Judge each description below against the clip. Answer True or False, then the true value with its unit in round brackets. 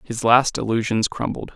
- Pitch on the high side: False (115 Hz)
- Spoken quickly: False (155 wpm)